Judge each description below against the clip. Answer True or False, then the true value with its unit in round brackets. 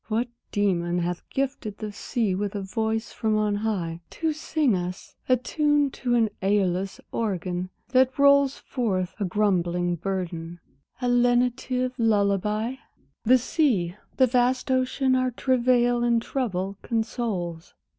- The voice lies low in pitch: False (220 Hz)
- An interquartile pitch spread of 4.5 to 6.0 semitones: True (5.1 semitones)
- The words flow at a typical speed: False (130 wpm)